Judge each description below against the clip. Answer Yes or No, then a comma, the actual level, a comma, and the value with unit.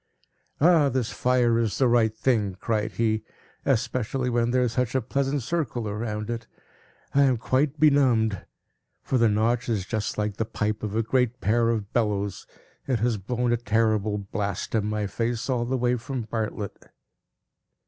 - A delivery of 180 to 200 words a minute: No, average, 170 wpm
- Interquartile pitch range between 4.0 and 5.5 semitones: No, average, 2.9 semitones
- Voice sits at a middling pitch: No, low, 115 Hz